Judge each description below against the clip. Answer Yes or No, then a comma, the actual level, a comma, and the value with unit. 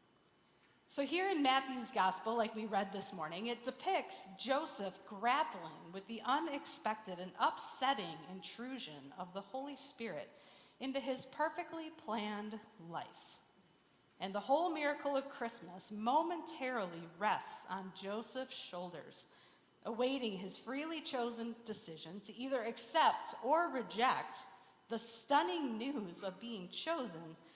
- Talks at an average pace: No, slow, 120 wpm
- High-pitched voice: Yes, high, 230 Hz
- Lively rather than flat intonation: Yes, wide, 5.9 semitones